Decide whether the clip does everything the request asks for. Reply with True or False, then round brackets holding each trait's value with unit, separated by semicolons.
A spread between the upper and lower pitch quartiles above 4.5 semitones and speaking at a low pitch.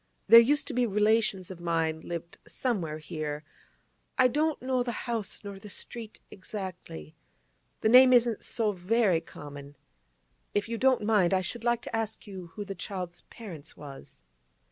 False (5.5 semitones; 205 Hz)